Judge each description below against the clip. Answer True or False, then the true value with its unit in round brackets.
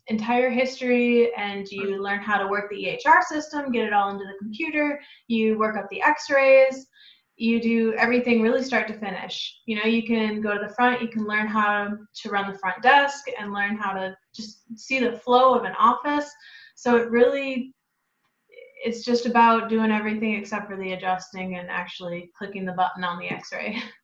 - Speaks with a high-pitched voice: True (225 Hz)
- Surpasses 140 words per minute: True (195 wpm)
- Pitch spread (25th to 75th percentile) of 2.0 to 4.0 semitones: True (3.6 semitones)